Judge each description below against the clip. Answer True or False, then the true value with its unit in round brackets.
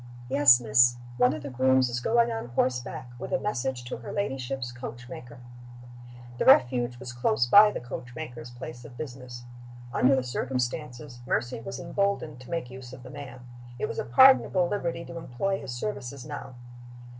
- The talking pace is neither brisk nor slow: True (180 wpm)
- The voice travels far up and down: False (3.6 semitones)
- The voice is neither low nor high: False (125 Hz)